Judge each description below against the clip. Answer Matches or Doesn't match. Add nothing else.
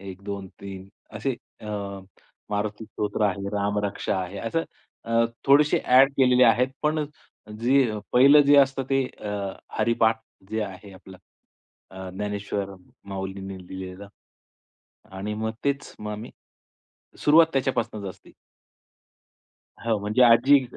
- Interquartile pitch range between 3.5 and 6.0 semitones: Matches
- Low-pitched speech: Matches